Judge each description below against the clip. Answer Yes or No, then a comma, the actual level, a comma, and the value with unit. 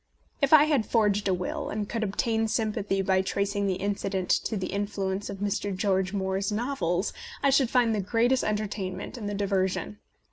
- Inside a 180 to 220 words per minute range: Yes, average, 185 wpm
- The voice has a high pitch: Yes, high, 205 Hz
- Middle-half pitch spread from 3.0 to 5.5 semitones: No, narrow, 2.6 semitones